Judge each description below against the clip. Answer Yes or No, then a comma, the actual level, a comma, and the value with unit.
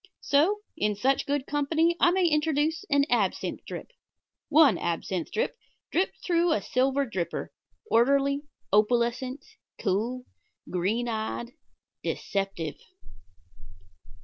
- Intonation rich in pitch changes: Yes, wide, 5.8 semitones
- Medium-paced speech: No, slow, 105 wpm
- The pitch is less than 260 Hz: No, very high, 270 Hz